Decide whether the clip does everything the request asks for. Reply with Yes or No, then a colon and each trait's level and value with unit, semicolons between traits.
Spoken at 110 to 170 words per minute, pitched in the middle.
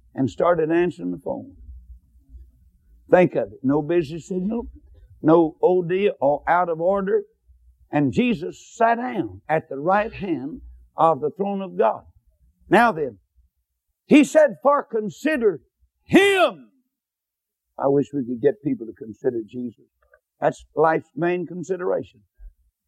Yes: slow, 135 wpm; medium, 160 Hz